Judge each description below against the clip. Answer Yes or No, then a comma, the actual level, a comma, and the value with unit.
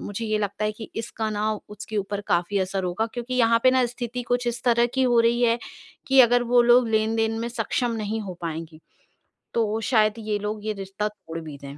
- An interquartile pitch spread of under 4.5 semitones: Yes, average, 2.8 semitones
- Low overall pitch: No, high, 220 Hz